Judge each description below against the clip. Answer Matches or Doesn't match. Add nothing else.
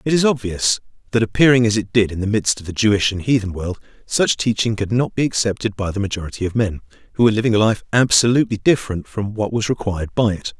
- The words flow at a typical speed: Doesn't match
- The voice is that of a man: Matches